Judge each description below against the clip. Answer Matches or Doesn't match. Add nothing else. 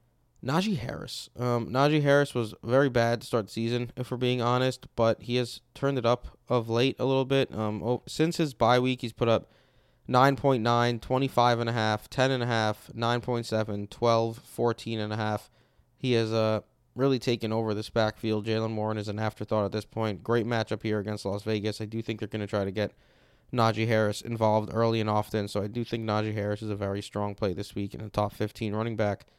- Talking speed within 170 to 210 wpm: Matches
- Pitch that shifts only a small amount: Matches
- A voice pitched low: Matches